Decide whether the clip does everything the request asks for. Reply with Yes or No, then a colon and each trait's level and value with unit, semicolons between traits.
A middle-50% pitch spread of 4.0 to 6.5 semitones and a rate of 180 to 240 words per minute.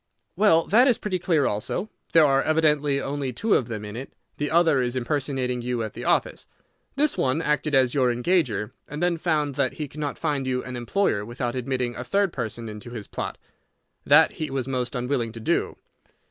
Yes: average, 4.3 semitones; average, 200 wpm